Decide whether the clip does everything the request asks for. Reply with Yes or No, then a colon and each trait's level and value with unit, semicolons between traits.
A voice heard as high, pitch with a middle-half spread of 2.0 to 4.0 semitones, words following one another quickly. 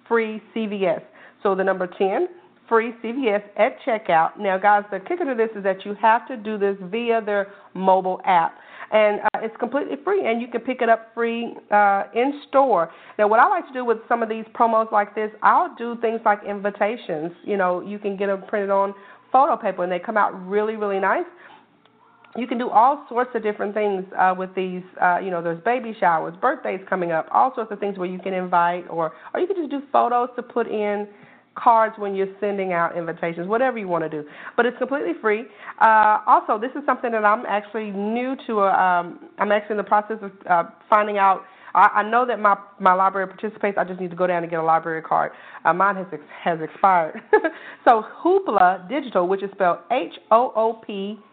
Yes: high, 210 Hz; average, 3.6 semitones; fast, 215 wpm